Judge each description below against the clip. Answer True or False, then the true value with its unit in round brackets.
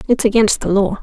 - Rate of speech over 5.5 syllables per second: True (5.8 syllables/s)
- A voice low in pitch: False (215 Hz)